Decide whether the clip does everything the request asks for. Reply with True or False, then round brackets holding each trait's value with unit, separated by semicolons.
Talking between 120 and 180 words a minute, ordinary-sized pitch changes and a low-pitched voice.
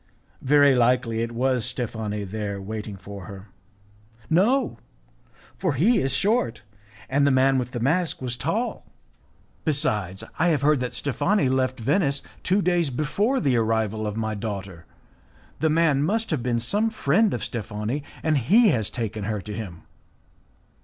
False (160 wpm; 6.3 semitones; 130 Hz)